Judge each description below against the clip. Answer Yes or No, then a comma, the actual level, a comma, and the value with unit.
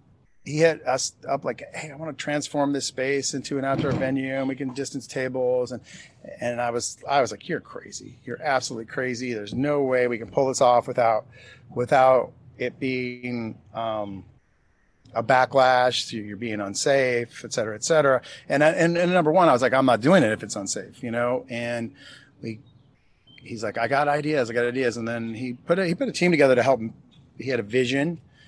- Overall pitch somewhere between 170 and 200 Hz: No, low, 130 Hz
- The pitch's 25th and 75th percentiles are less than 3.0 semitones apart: Yes, narrow, 2.5 semitones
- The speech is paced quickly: Yes, fast, 210 wpm